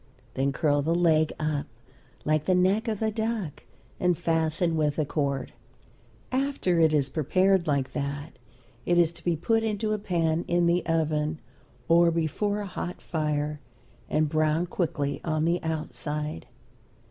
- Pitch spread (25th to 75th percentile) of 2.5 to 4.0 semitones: Yes, average, 2.8 semitones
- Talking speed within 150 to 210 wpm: Yes, average, 155 wpm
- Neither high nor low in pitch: Yes, medium, 160 Hz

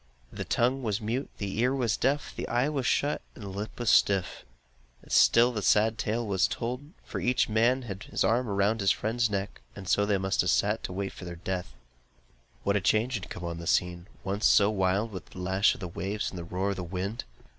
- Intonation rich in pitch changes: No, average, 3.6 semitones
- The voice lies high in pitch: No, low, 105 Hz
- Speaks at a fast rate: Yes, fast, 220 wpm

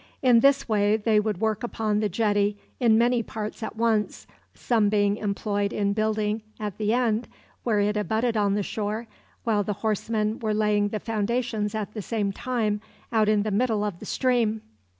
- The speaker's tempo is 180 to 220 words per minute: Yes, average, 185 wpm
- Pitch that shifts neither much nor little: No, narrow, 1.5 semitones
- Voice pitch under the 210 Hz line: No, high, 215 Hz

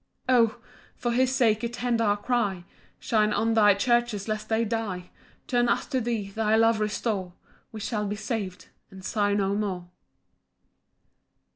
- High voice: Yes, high, 215 Hz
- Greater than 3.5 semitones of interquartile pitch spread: No, narrow, 2.4 semitones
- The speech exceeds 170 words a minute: No, average, 155 wpm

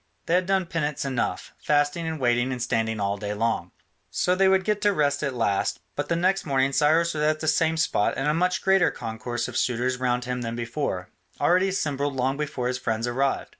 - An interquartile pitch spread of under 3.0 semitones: No, average, 5.3 semitones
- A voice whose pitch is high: No, medium, 140 Hz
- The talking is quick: Yes, fast, 215 wpm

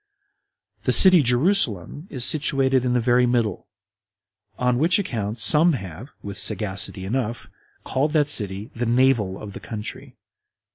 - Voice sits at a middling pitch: No, low, 125 Hz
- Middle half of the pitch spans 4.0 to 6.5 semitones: Yes, average, 4.6 semitones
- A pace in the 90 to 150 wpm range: Yes, average, 140 wpm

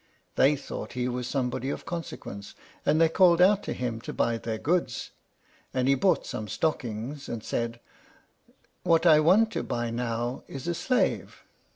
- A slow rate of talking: No, average, 170 wpm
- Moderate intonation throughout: No, wide, 5.9 semitones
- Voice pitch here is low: Yes, low, 130 Hz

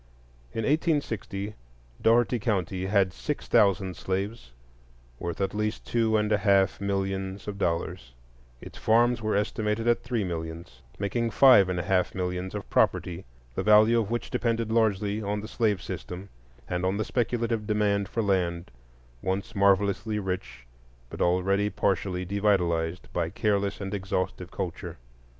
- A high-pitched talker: No, low, 100 Hz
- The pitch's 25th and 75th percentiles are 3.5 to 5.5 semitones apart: No, average, 2.7 semitones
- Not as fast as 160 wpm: Yes, average, 145 wpm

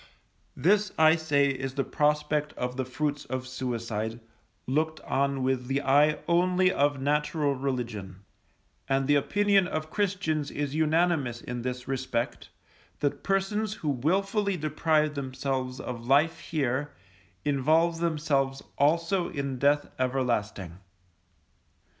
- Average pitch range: Yes, average, 3.5 semitones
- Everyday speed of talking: No, slow, 125 wpm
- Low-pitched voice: No, medium, 145 Hz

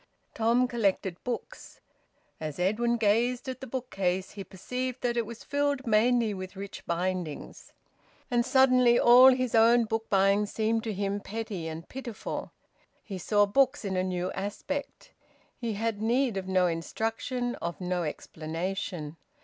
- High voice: Yes, high, 220 Hz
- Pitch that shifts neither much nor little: Yes, average, 4.5 semitones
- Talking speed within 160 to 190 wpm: No, average, 150 wpm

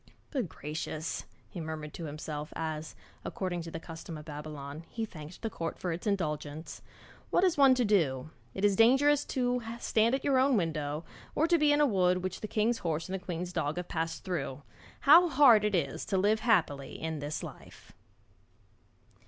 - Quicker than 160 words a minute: Yes, average, 190 wpm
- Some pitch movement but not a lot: No, wide, 6.6 semitones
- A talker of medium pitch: Yes, medium, 175 Hz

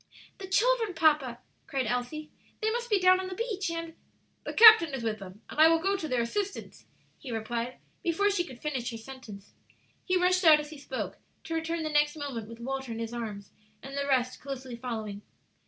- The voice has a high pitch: Yes, very high, 295 Hz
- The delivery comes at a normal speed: No, fast, 210 wpm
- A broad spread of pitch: Yes, wide, 7.1 semitones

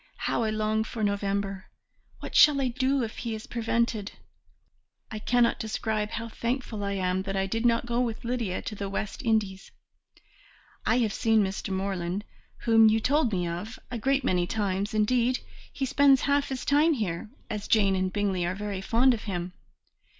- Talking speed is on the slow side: No, average, 180 wpm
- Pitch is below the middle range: No, high, 220 Hz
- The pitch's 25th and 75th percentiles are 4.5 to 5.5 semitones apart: No, average, 3.4 semitones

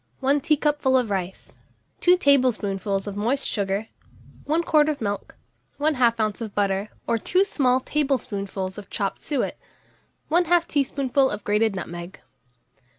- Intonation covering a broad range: Yes, wide, 6.1 semitones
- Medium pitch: No, high, 240 Hz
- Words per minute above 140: No, slow, 135 wpm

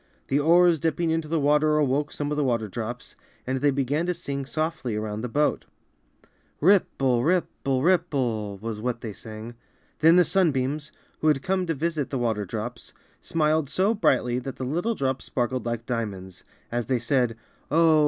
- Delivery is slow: No, average, 180 wpm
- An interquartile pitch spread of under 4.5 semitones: No, average, 4.8 semitones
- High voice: No, low, 135 Hz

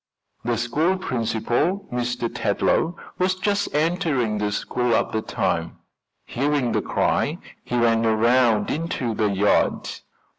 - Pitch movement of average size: No, wide, 6.2 semitones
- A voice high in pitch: No, low, 120 Hz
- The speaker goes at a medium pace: No, slow, 125 wpm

